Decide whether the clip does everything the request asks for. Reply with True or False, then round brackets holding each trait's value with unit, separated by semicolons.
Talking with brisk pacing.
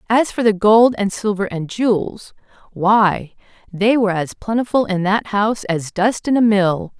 False (170 wpm)